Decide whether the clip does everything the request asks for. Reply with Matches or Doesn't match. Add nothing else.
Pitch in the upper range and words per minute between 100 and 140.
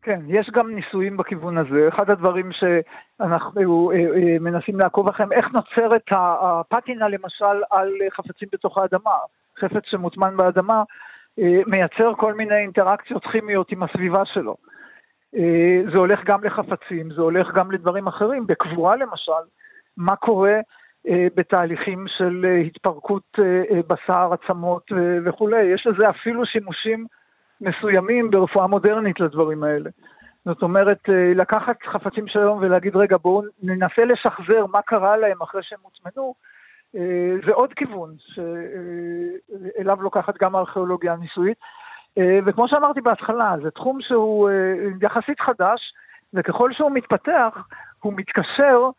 Matches